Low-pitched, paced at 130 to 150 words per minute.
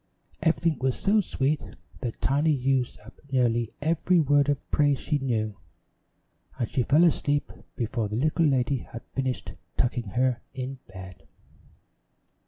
Yes: low, 130 Hz; average, 140 wpm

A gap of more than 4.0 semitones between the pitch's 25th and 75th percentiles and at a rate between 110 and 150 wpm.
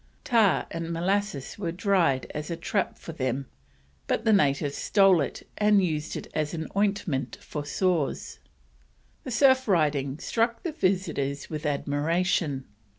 Yes: wide, 5.6 semitones; average, 140 wpm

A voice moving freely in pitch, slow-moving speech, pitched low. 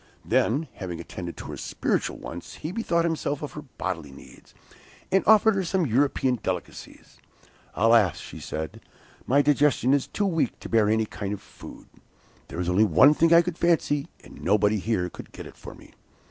No: wide, 8.6 semitones; average, 185 wpm; low, 130 Hz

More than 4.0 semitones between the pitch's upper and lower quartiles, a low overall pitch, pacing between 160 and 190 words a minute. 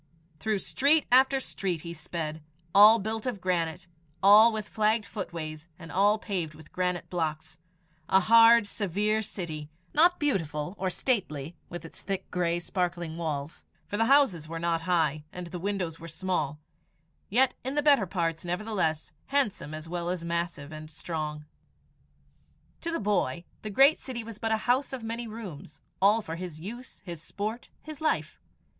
No: average, 5.2 semitones; medium, 185 Hz; average, 165 wpm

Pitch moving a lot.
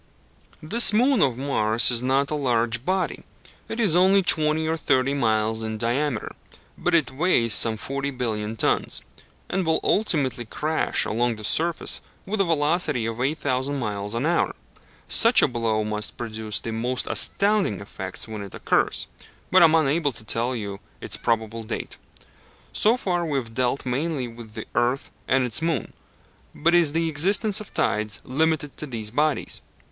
Yes: wide, 6.0 semitones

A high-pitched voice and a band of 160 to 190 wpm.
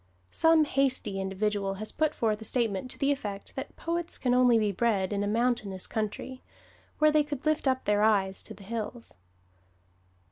Yes: high, 225 Hz; average, 180 wpm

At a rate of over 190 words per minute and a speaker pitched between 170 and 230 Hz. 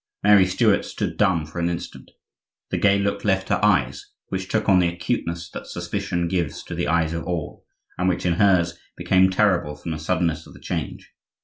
No: average, 200 wpm; very low, 90 Hz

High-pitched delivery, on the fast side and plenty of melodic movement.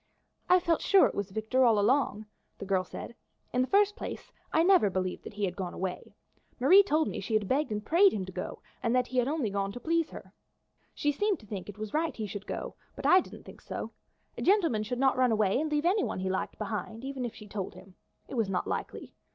Yes: high, 235 Hz; fast, 245 wpm; wide, 7.2 semitones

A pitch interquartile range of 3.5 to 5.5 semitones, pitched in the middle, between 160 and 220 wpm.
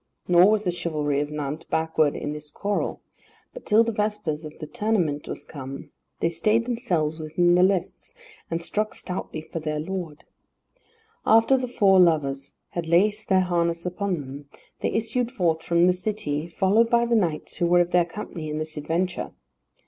Yes: average, 5.1 semitones; medium, 175 Hz; average, 180 wpm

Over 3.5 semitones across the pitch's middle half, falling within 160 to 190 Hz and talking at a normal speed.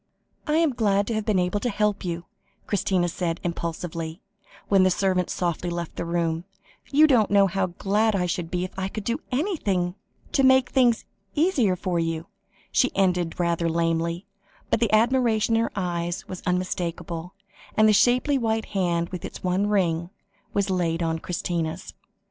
Yes: average, 4.1 semitones; medium, 185 Hz; average, 170 wpm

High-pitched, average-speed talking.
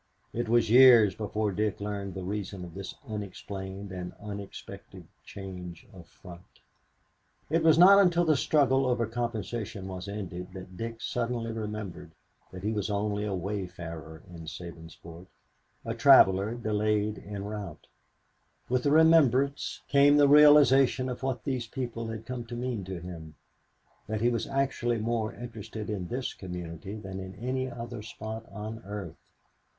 No: low, 105 Hz; average, 150 wpm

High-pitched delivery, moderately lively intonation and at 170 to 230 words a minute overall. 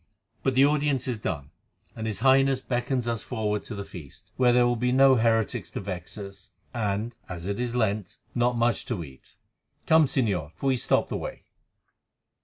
No: low, 115 Hz; average, 4.2 semitones; average, 190 wpm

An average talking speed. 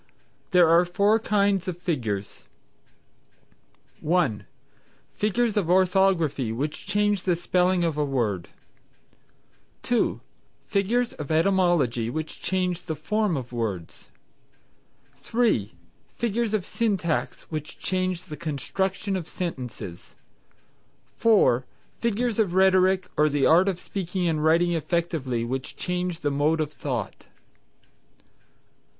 No: slow, 115 wpm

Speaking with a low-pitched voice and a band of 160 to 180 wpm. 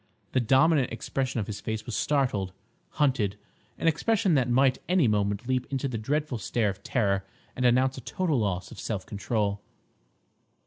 Yes: low, 120 Hz; average, 165 wpm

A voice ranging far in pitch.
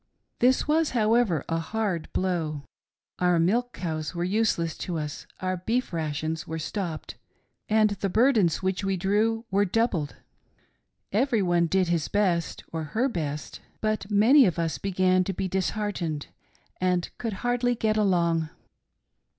No: average, 4.6 semitones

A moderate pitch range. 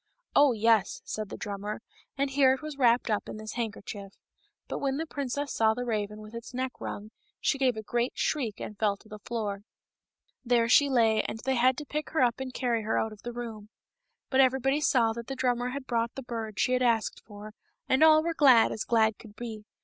Yes: average, 3.4 semitones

